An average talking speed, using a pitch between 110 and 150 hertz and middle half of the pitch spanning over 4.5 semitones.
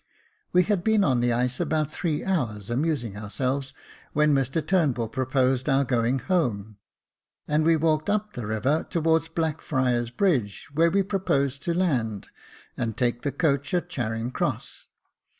Yes: average, 155 wpm; medium, 140 Hz; average, 5.3 semitones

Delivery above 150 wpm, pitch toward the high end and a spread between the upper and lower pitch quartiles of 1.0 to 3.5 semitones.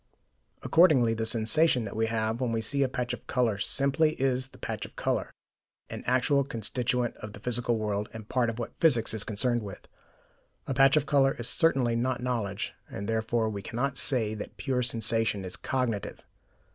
No: average, 185 wpm; low, 120 Hz; average, 2.8 semitones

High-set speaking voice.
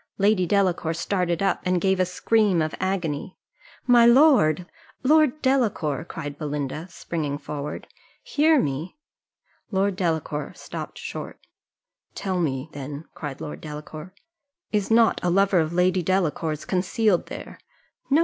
No: medium, 180 Hz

